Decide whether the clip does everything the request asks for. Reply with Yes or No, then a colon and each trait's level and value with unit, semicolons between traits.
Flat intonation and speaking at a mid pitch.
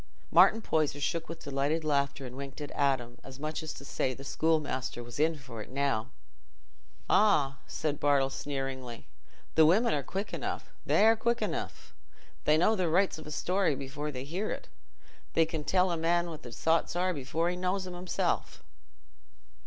No: average, 4.1 semitones; medium, 155 Hz